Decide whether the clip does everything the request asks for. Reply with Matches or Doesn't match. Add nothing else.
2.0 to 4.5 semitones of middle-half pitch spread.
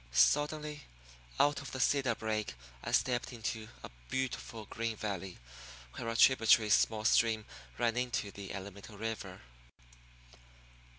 Matches